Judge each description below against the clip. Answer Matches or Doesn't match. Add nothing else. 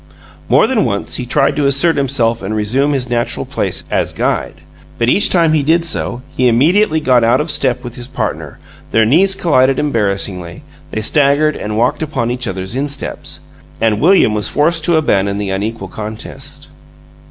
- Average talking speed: Matches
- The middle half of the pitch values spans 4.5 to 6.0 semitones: Matches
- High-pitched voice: Doesn't match